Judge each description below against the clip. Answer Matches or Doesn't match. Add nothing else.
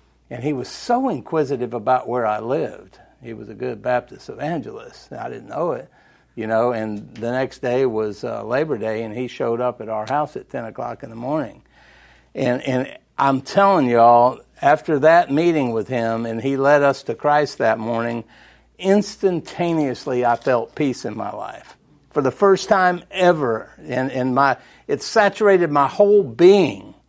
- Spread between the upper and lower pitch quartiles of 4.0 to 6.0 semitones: Matches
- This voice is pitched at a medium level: Doesn't match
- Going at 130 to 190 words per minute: Matches